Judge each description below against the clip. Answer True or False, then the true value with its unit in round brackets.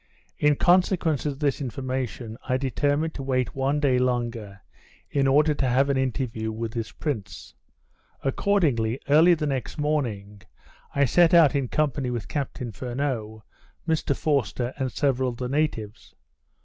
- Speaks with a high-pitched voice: False (135 Hz)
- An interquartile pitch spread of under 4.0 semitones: True (3.5 semitones)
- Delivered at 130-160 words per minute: True (150 wpm)